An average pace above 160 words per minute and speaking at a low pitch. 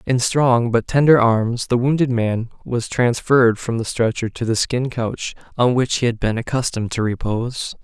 Yes: average, 190 wpm; low, 120 Hz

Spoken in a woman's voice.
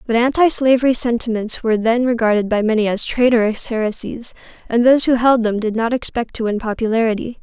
Yes: female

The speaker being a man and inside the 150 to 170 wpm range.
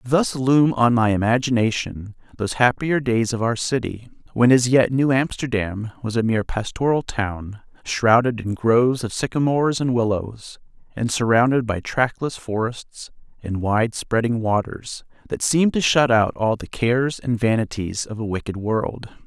Yes: male; average, 160 wpm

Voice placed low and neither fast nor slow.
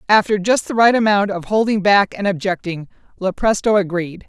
No: high, 200 Hz; average, 170 wpm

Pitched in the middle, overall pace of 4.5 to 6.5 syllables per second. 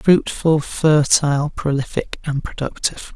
No: medium, 150 Hz; 4.2 syllables/s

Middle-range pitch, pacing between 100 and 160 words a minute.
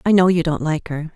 No: medium, 165 Hz; fast, 310 wpm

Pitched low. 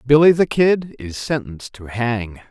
Yes: low, 125 Hz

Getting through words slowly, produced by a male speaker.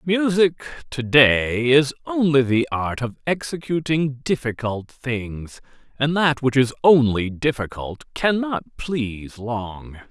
Yes: slow, 120 wpm; male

